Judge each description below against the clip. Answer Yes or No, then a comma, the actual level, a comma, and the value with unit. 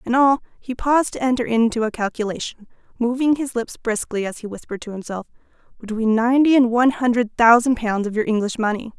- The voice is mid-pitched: No, high, 235 Hz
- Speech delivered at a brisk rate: No, average, 185 wpm